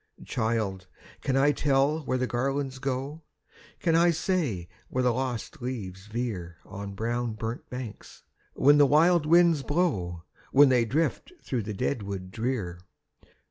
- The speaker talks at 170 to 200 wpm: No, average, 150 wpm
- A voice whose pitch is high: No, low, 125 Hz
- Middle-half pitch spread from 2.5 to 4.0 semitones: No, average, 5.1 semitones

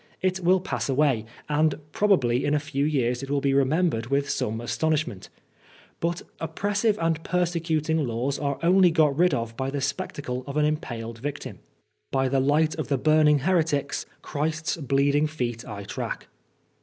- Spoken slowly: No, average, 160 wpm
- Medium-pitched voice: Yes, medium, 145 Hz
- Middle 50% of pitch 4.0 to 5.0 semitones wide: No, average, 3.4 semitones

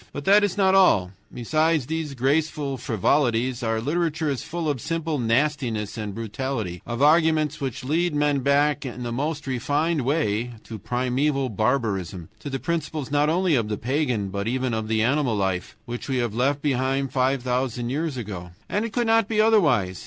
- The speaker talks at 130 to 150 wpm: No, average, 190 wpm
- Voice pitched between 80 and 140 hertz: Yes, low, 135 Hz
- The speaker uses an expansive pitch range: No, average, 4.6 semitones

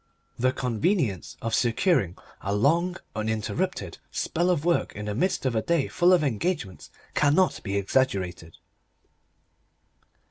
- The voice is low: Yes, low, 130 Hz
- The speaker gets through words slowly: Yes, slow, 130 wpm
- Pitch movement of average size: No, wide, 8.8 semitones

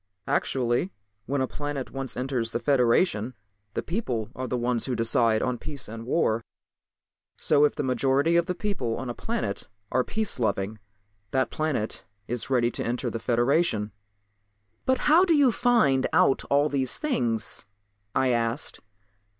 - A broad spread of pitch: No, average, 4.2 semitones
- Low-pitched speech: Yes, low, 130 Hz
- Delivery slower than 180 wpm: Yes, average, 160 wpm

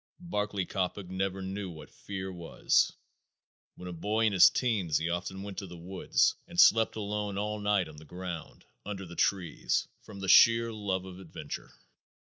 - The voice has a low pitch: Yes, very low, 95 Hz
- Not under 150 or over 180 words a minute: Yes, average, 175 wpm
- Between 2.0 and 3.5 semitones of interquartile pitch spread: Yes, narrow, 2.5 semitones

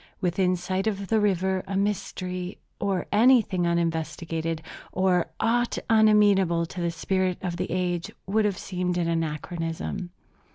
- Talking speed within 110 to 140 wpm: Yes, slow, 135 wpm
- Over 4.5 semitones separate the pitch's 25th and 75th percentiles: No, narrow, 2.6 semitones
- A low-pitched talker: No, medium, 185 Hz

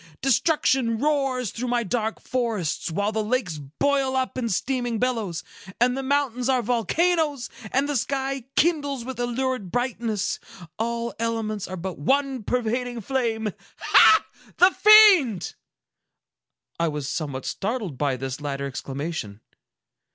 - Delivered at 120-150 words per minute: Yes, slow, 135 wpm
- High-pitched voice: Yes, high, 240 Hz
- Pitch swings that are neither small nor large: Yes, average, 5.0 semitones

